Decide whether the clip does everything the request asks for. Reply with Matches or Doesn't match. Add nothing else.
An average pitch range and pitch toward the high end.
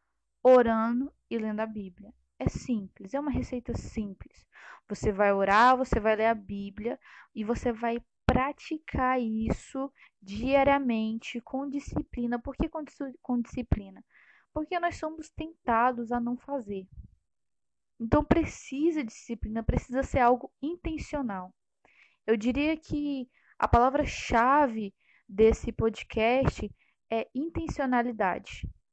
Matches